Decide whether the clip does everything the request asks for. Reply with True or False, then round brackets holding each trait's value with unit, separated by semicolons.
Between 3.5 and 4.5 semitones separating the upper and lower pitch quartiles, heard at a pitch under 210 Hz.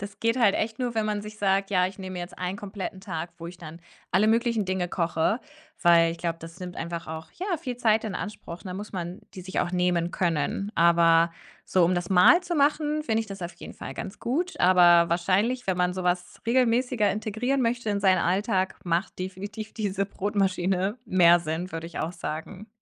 True (3.8 semitones; 190 Hz)